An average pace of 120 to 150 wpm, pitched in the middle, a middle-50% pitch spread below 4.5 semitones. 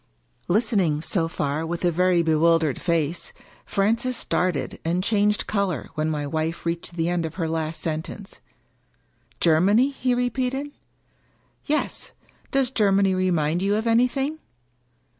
No: average, 140 wpm; medium, 180 Hz; average, 5.1 semitones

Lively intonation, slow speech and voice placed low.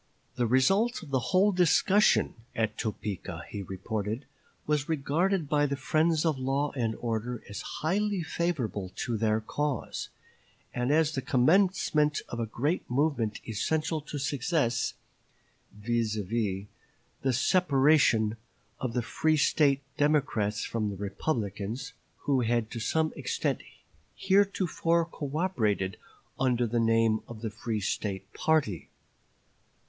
Yes: wide, 6.1 semitones; slow, 125 wpm; low, 130 Hz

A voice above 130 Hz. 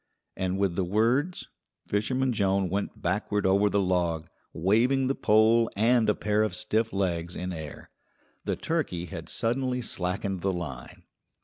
No: low, 100 Hz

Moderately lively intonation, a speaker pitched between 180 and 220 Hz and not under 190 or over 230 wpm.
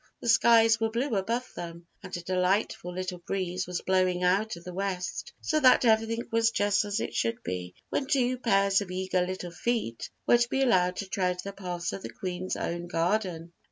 Yes: average, 3.9 semitones; high, 190 Hz; average, 200 wpm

